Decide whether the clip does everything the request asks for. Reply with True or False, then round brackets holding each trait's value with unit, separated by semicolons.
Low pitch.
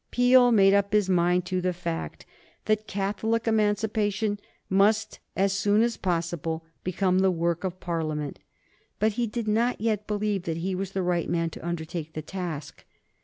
False (195 Hz)